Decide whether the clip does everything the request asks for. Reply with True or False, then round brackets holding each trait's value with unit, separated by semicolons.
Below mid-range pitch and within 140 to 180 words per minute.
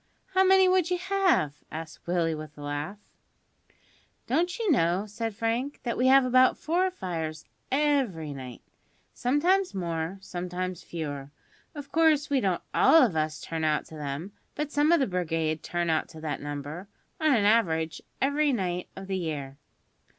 False (190 Hz; 165 wpm)